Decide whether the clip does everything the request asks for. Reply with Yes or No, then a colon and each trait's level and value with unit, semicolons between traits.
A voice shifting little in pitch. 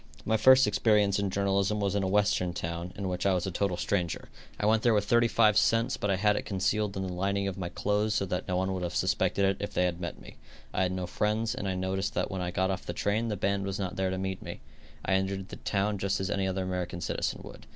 Yes: narrow, 1.9 semitones